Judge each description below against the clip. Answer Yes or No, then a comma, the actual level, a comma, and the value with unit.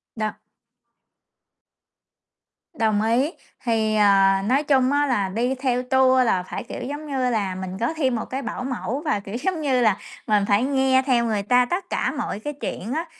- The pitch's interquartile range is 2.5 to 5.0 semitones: Yes, average, 3.8 semitones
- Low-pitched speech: No, very high, 250 Hz